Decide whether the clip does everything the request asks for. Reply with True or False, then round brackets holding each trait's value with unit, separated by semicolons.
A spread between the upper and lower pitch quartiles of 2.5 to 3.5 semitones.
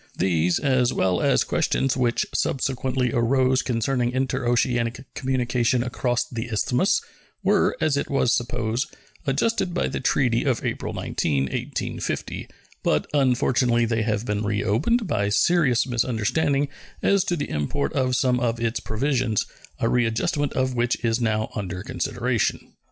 True (2.8 semitones)